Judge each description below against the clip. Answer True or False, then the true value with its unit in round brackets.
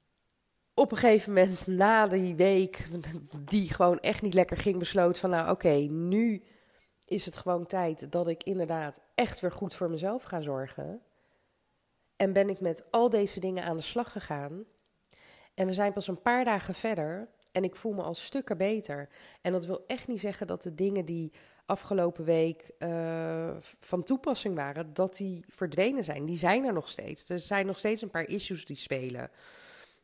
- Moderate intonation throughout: True (3.5 semitones)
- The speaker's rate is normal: True (185 wpm)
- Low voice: False (185 Hz)